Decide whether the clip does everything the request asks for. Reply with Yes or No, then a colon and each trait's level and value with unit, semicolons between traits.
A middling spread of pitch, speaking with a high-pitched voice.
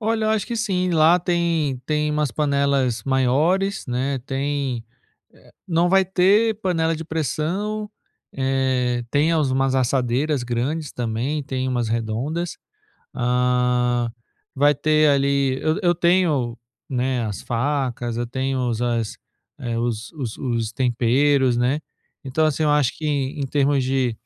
No: average, 4.1 semitones; low, 135 Hz